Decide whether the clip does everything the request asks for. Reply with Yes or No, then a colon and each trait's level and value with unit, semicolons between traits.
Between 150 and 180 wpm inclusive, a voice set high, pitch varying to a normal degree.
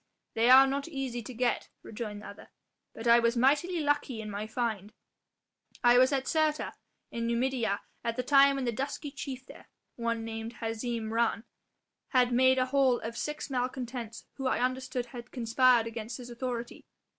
No: average, 175 wpm; high, 245 Hz; narrow, 2.3 semitones